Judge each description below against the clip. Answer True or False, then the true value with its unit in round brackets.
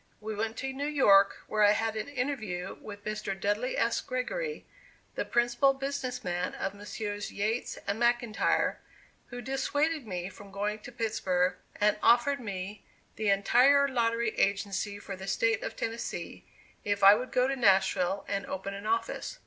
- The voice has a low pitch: False (220 Hz)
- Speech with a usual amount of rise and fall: True (3.9 semitones)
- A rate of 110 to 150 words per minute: False (165 wpm)